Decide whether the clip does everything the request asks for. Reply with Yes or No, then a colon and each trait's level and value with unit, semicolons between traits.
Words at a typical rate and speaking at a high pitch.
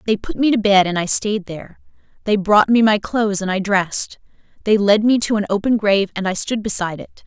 No: fast, 240 wpm; high, 205 Hz